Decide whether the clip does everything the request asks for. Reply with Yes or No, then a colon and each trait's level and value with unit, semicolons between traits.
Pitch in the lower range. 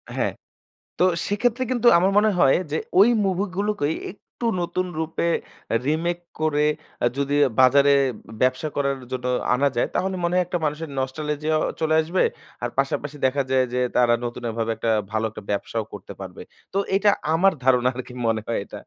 No: medium, 145 Hz